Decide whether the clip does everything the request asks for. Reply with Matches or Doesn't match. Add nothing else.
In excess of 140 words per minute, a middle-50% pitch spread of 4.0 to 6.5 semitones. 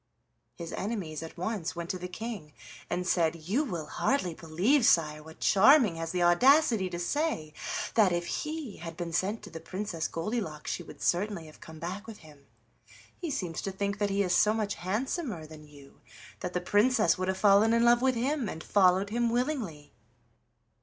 Matches